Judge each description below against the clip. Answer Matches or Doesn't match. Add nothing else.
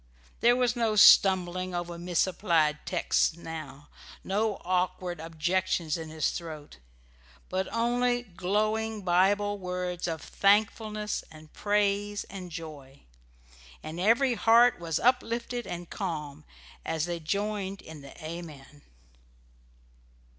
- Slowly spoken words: Matches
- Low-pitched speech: Doesn't match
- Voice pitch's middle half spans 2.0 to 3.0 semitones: Doesn't match